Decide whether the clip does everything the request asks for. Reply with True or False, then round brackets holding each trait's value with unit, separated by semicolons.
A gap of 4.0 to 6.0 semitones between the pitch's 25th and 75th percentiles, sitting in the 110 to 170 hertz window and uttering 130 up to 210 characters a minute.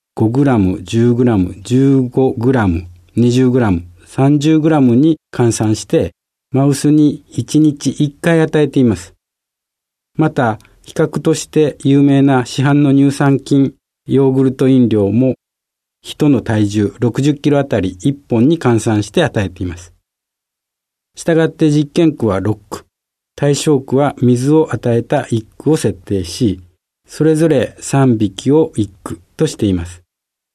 True (5.3 semitones; 130 Hz; 205 characters per minute)